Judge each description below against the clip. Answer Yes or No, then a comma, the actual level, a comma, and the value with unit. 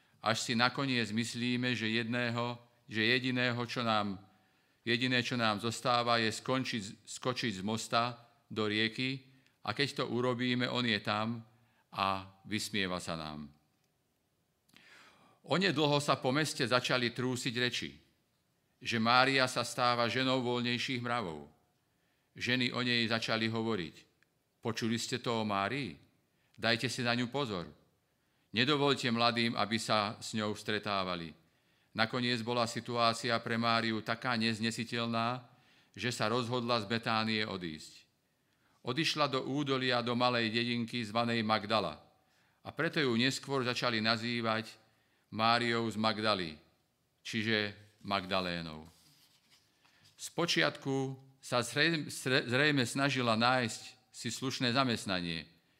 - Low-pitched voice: Yes, low, 120 Hz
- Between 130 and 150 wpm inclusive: No, average, 115 wpm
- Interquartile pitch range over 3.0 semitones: No, narrow, 2.4 semitones